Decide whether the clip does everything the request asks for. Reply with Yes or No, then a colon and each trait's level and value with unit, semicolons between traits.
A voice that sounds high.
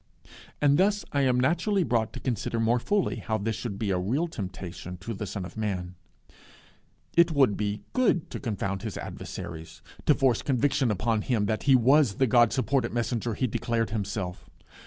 No: low, 115 Hz